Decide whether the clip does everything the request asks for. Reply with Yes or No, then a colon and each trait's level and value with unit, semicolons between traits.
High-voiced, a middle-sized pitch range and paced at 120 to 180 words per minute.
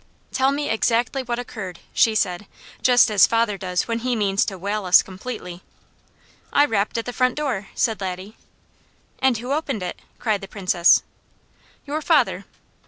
Yes: high, 220 Hz; average, 4.2 semitones; average, 165 wpm